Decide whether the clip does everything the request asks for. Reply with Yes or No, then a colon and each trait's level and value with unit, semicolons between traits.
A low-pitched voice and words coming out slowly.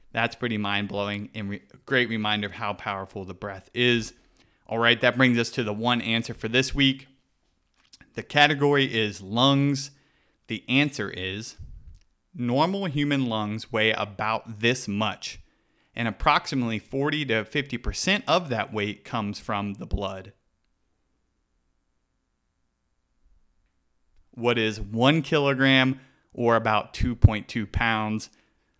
Yes: low, 110 Hz; slow, 125 wpm